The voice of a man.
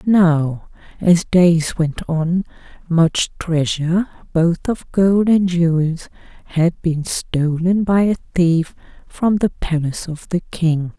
No: female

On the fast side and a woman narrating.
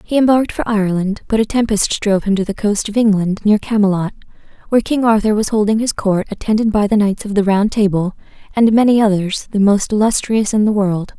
Yes: fast, 215 wpm; female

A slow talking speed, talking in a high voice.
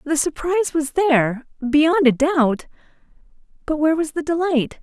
Yes: slow, 125 wpm; very high, 300 Hz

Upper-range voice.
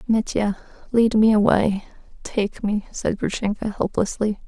Yes: high, 210 Hz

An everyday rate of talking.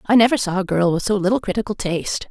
No: fast, 260 wpm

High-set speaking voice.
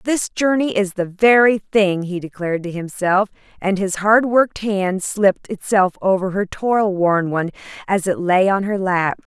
Yes: high, 195 Hz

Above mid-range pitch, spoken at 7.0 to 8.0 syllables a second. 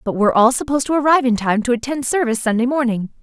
Yes: high, 245 Hz; 7.5 syllables/s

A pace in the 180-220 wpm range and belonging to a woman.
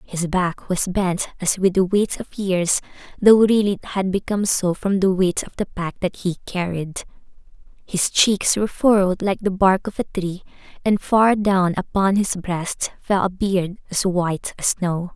Yes: average, 190 wpm; female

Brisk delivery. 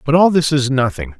Yes: fast, 250 wpm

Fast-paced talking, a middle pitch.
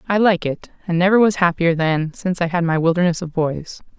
Yes: fast, 225 wpm; medium, 175 Hz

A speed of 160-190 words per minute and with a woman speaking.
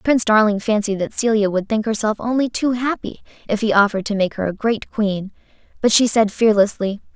No: average, 200 wpm; female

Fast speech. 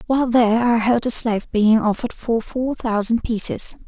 No: average, 185 wpm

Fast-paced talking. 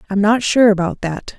Yes: fast, 215 wpm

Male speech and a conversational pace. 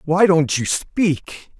Yes: male; average, 150 wpm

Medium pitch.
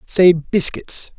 Yes: medium, 175 Hz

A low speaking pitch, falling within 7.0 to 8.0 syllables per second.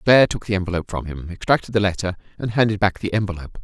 Yes: low, 100 Hz; 7.5 syllables/s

